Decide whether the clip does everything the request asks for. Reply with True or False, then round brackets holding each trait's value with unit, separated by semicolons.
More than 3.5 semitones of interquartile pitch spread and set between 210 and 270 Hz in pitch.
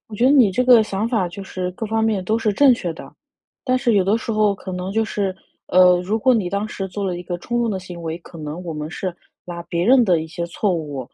False (4.0 semitones; 195 Hz)